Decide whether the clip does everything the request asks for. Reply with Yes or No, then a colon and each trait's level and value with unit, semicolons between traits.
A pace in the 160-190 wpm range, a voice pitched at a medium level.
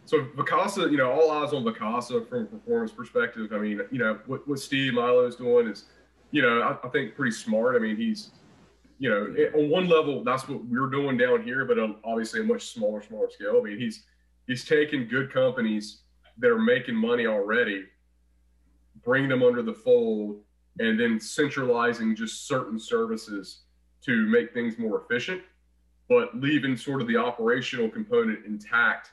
Yes: average, 180 wpm; medium, 155 Hz